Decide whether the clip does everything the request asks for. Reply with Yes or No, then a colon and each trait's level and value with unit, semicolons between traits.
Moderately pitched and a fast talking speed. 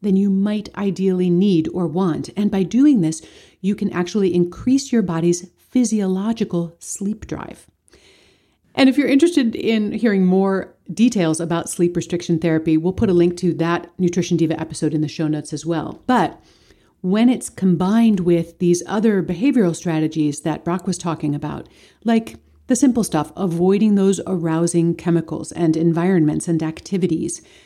No: medium, 180 Hz; average, 160 wpm